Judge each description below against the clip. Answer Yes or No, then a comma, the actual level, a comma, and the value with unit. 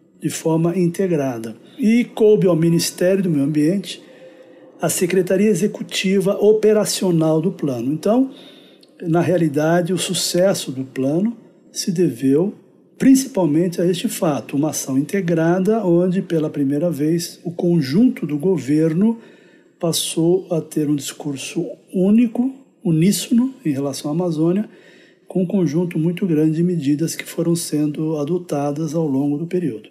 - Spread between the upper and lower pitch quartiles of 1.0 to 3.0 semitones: No, average, 3.6 semitones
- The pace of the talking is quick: No, average, 130 wpm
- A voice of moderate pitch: Yes, medium, 175 Hz